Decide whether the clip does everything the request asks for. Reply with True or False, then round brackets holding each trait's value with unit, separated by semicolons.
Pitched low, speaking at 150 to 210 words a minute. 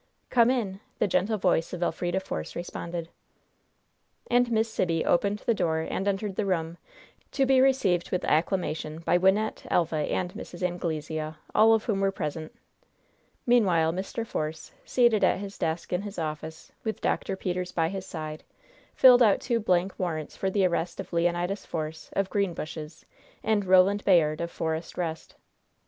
False (180 Hz; 160 wpm)